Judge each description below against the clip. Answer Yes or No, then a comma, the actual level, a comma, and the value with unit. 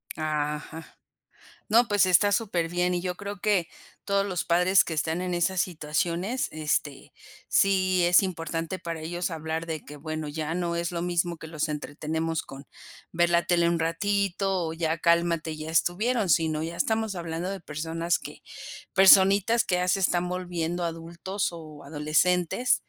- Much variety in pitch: No, narrow, 2.4 semitones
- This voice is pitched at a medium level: Yes, medium, 170 Hz